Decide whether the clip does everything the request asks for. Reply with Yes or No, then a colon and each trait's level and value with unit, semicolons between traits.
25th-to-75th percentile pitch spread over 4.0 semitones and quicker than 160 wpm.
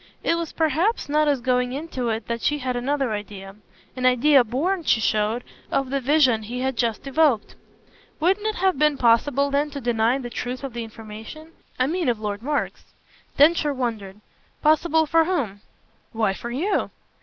Yes: average, 4.6 semitones; average, 180 wpm